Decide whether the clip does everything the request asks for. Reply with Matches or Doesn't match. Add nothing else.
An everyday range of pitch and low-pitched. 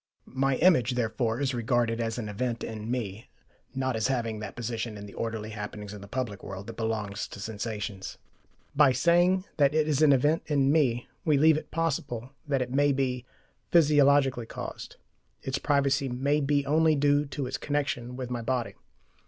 Matches